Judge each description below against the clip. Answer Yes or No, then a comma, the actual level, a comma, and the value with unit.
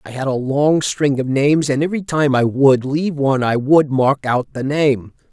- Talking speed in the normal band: No, fast, 225 wpm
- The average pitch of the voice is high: No, medium, 140 Hz